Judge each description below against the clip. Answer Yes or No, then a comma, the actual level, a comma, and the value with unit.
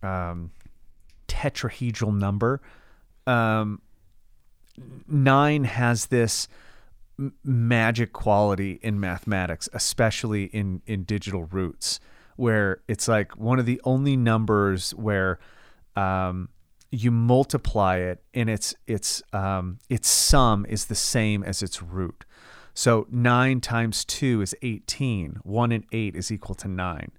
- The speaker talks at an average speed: No, slow, 120 wpm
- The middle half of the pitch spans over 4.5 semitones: No, average, 3.9 semitones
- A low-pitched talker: Yes, low, 105 Hz